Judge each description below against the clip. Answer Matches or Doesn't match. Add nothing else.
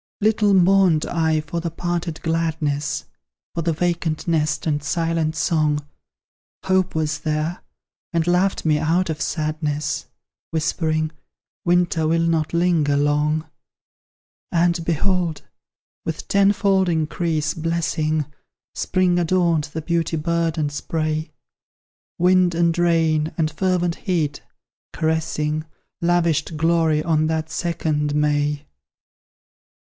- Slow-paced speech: Matches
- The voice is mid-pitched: Matches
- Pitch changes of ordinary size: Doesn't match